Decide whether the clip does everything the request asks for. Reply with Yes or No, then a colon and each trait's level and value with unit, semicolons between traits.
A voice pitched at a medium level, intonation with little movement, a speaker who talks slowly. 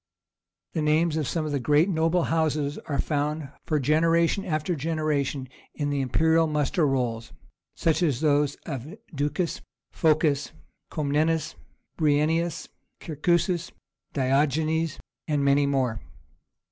Yes: medium, 150 Hz; narrow, 2.3 semitones; slow, 120 wpm